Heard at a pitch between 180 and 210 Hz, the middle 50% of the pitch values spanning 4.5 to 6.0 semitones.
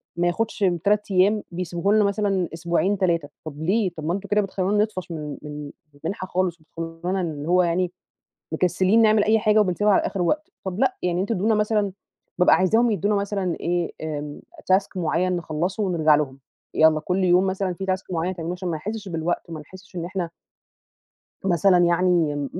No: medium, 185 Hz; average, 3.1 semitones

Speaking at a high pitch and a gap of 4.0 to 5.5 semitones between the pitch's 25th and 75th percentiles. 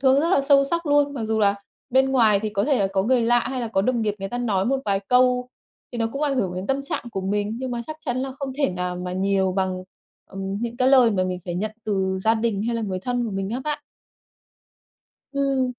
Yes: high, 230 Hz; average, 5.2 semitones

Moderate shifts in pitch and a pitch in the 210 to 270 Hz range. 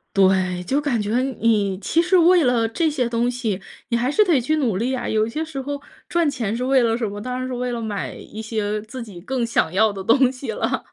Yes: average, 3.7 semitones; high, 235 Hz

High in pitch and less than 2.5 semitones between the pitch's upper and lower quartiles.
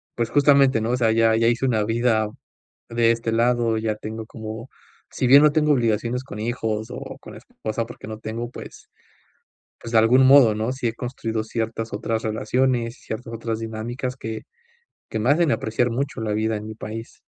No: low, 115 Hz; narrow, 2.0 semitones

